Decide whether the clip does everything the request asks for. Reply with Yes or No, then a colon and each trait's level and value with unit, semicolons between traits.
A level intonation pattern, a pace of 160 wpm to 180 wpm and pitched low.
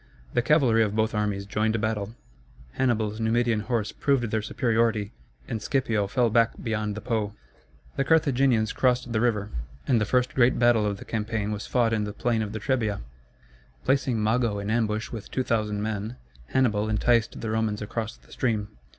Yes: narrow, 2.2 semitones; average, 175 wpm; low, 110 Hz